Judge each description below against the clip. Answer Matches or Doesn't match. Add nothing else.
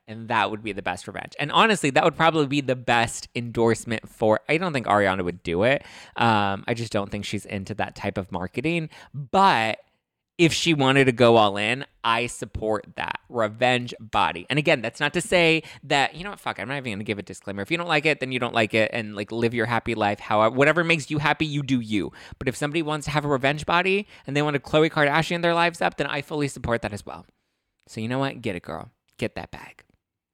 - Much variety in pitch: Matches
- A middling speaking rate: Doesn't match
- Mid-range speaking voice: Doesn't match